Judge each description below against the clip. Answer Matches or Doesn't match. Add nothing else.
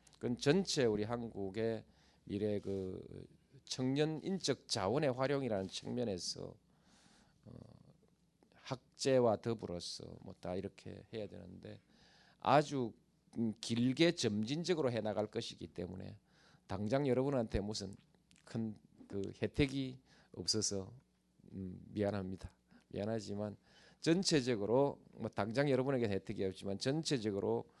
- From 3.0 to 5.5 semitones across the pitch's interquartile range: Matches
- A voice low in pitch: Matches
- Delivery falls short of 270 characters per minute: Matches